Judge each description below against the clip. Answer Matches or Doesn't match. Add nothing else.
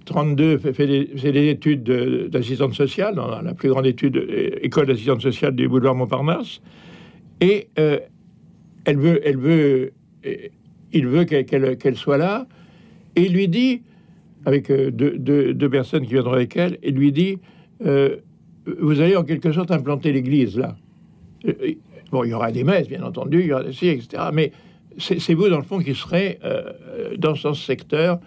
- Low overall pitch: Doesn't match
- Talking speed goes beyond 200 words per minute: Doesn't match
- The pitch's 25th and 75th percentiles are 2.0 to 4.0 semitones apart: Doesn't match